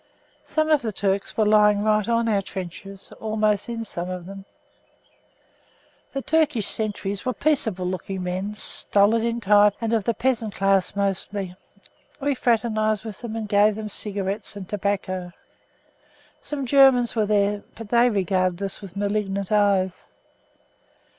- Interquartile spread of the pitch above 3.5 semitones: No, narrow, 2.6 semitones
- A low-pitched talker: No, high, 210 Hz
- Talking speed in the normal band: Yes, average, 145 wpm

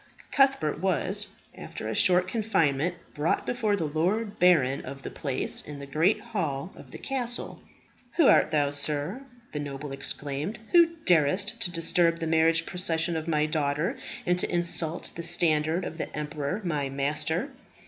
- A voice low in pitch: No, medium, 165 Hz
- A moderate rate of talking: Yes, average, 160 wpm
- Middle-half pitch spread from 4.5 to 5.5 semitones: No, average, 3.8 semitones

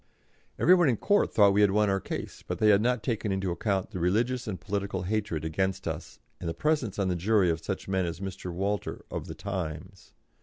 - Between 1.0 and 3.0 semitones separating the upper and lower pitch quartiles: Yes, narrow, 2.6 semitones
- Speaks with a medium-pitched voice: No, low, 100 Hz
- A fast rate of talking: Yes, fast, 230 wpm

